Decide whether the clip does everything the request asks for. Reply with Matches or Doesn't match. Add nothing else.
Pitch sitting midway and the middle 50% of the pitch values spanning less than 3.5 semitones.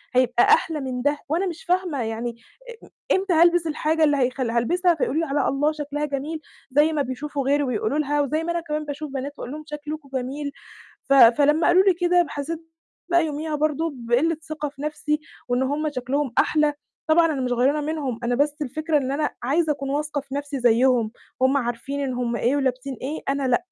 Doesn't match